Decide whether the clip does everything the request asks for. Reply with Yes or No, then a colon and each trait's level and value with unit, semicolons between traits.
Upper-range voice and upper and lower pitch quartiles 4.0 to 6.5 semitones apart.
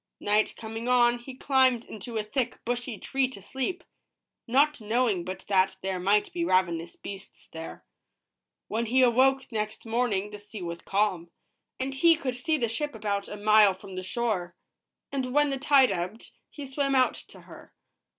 Yes: high, 230 Hz; average, 4.6 semitones